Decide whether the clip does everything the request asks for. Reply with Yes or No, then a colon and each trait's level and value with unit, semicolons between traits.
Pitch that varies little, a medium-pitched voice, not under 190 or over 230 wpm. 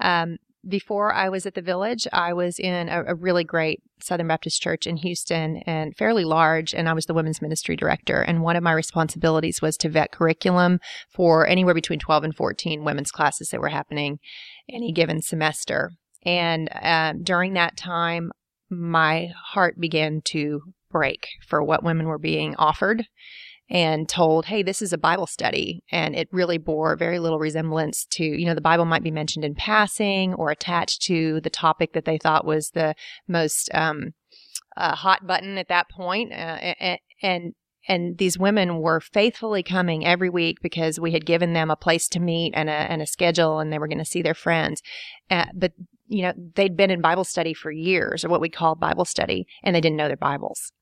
Yes: narrow, 2.2 semitones; medium, 170 Hz; average, 195 wpm